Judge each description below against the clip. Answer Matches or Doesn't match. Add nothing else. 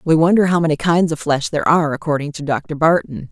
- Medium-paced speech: Doesn't match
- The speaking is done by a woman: Matches